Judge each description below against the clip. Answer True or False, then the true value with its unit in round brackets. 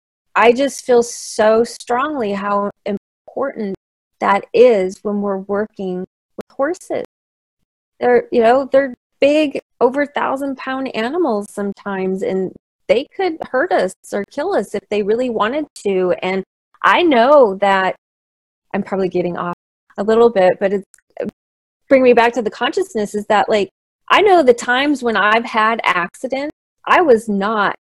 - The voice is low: False (220 Hz)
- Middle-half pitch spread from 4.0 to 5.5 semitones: True (4.9 semitones)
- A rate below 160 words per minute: True (150 wpm)